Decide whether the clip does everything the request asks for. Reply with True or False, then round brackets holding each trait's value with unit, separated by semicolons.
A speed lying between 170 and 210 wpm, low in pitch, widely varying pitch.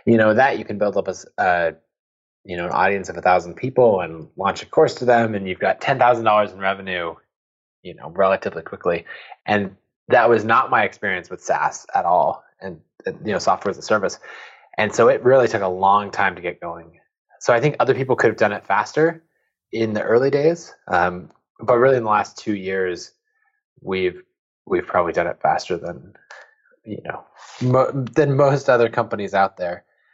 True (205 wpm; 115 Hz; 8.7 semitones)